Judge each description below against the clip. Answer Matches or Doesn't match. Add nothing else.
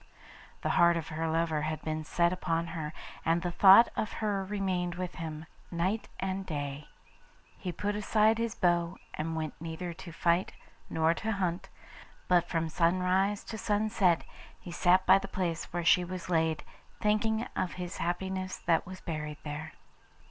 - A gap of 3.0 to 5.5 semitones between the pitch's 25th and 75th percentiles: Doesn't match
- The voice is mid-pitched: Matches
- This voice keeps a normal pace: Matches